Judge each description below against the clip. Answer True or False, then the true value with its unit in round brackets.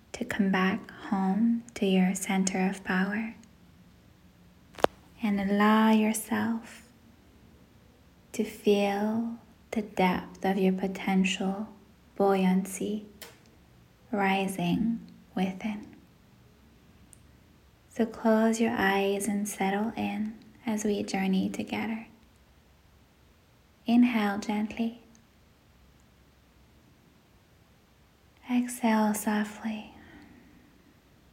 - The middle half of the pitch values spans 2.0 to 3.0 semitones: True (2.5 semitones)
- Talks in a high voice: True (210 Hz)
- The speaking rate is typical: False (70 wpm)